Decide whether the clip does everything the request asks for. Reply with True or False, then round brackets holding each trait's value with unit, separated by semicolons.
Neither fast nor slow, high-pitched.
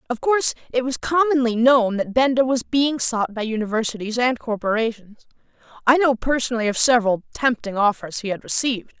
True (165 wpm; 240 Hz)